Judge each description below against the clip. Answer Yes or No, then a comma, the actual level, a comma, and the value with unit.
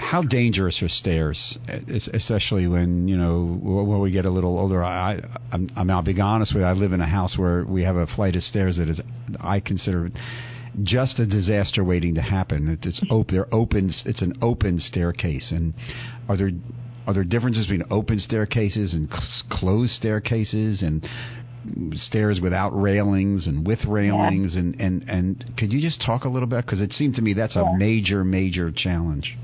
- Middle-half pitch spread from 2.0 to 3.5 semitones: No, average, 4.0 semitones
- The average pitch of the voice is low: Yes, low, 100 Hz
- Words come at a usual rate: Yes, average, 185 wpm